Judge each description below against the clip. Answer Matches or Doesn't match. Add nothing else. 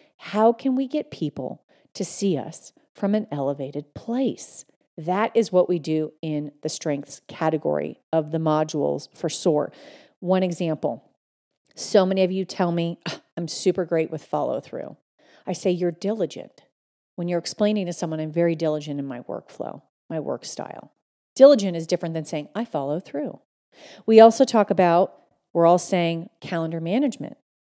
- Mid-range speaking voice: Matches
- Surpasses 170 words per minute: Doesn't match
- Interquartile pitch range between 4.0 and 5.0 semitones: Matches